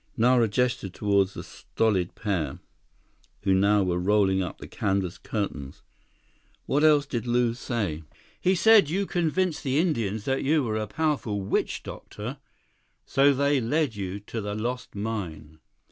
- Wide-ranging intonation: Yes, wide, 5.8 semitones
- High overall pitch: No, low, 110 Hz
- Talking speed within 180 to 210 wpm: No, average, 150 wpm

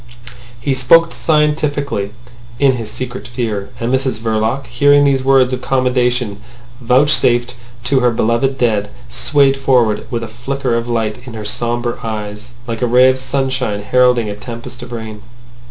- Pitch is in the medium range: No, low, 125 Hz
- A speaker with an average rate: Yes, average, 155 wpm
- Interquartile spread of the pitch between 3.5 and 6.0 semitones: No, average, 2.7 semitones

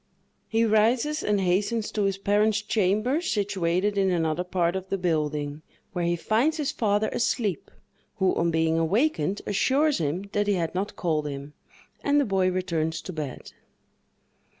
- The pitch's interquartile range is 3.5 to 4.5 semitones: Yes, average, 4.2 semitones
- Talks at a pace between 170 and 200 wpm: No, average, 160 wpm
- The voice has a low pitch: No, high, 190 Hz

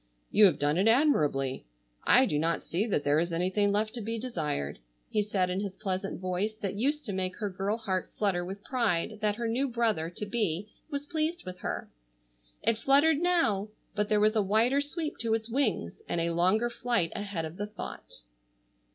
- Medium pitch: No, high, 210 Hz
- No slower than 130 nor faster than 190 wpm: No, average, 200 wpm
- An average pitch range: Yes, average, 4.4 semitones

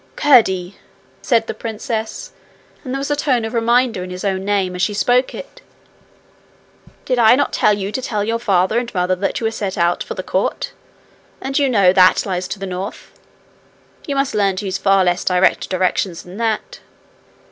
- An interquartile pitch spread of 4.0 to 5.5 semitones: Yes, average, 4.4 semitones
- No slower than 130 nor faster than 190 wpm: No, average, 200 wpm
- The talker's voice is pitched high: Yes, high, 210 Hz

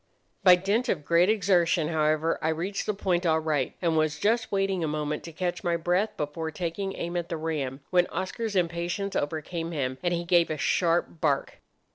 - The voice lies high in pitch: No, medium, 170 Hz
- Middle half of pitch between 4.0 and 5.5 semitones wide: No, average, 2.8 semitones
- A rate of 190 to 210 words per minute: Yes, average, 195 wpm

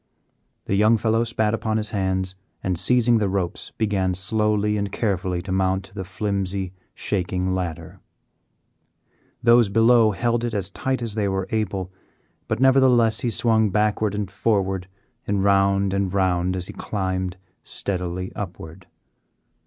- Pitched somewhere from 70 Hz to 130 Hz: Yes, low, 100 Hz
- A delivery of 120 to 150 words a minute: Yes, average, 145 wpm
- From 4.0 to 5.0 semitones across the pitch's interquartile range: No, average, 2.8 semitones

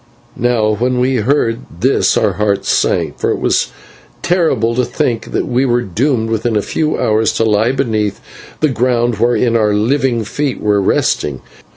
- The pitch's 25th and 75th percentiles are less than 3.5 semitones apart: Yes, average, 2.9 semitones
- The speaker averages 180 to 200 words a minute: No, average, 170 wpm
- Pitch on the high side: No, low, 115 Hz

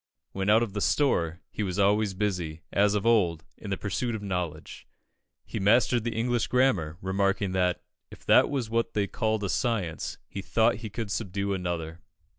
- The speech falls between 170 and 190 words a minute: Yes, average, 185 wpm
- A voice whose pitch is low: Yes, low, 100 Hz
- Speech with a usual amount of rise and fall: Yes, average, 3.6 semitones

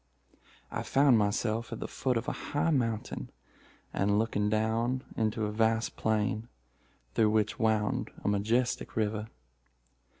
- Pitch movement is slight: Yes, narrow, 1.8 semitones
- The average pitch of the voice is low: Yes, low, 110 Hz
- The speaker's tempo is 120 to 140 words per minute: Yes, slow, 135 wpm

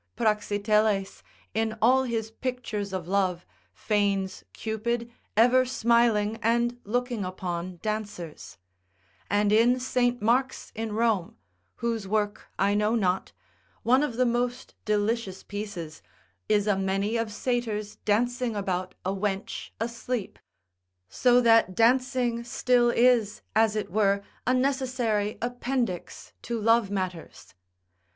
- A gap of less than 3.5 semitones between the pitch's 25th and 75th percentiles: Yes, average, 2.9 semitones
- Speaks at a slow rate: Yes, slow, 120 wpm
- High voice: Yes, high, 220 Hz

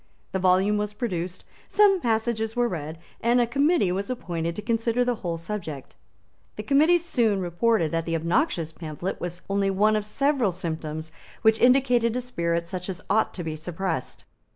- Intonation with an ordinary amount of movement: No, wide, 5.8 semitones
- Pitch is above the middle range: Yes, high, 200 Hz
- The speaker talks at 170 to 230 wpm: Yes, average, 175 wpm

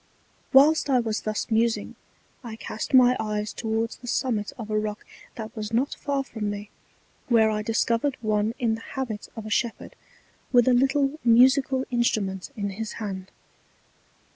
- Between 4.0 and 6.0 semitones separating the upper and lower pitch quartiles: No, average, 3.0 semitones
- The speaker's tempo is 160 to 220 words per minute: Yes, average, 165 wpm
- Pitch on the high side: Yes, high, 225 Hz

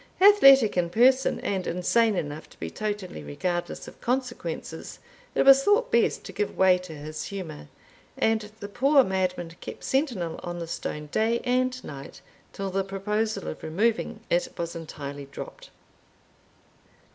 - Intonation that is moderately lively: No, wide, 5.9 semitones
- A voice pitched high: Yes, high, 195 Hz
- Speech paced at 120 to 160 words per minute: Yes, average, 150 wpm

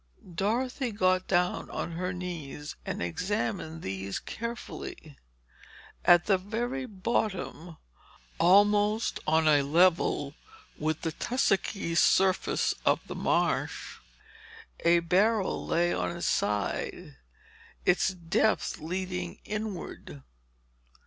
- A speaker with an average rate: No, slow, 100 wpm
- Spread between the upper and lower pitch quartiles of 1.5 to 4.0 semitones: No, average, 4.5 semitones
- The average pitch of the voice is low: No, medium, 180 Hz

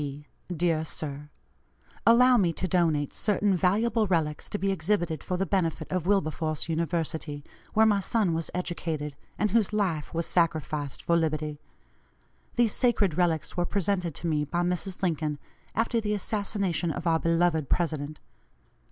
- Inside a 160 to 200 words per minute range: No, average, 150 wpm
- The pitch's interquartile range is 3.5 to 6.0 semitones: Yes, average, 4.1 semitones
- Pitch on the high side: No, medium, 170 Hz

